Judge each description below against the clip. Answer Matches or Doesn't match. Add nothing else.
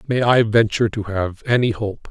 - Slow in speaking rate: Doesn't match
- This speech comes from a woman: Doesn't match